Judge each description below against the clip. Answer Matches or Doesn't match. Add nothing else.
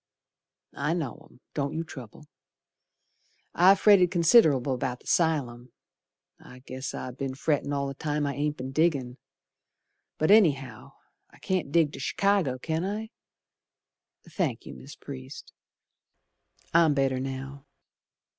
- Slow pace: Matches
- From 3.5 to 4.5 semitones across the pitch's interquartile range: Matches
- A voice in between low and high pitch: Matches